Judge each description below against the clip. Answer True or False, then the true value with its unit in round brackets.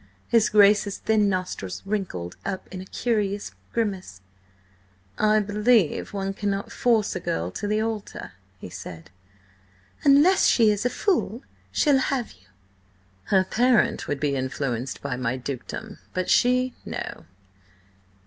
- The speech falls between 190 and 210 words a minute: False (135 wpm)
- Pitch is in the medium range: False (200 Hz)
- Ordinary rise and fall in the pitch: False (7.5 semitones)